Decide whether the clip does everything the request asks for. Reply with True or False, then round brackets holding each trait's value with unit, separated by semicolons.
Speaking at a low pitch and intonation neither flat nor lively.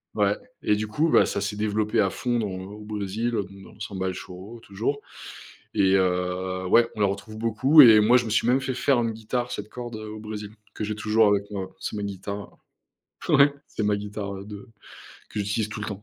False (105 Hz; 2.1 semitones)